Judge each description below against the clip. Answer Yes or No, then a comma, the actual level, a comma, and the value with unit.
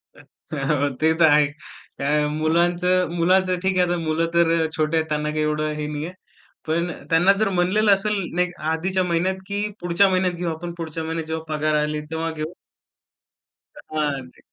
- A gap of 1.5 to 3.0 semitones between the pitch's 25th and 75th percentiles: Yes, average, 2.7 semitones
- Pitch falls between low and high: Yes, medium, 165 Hz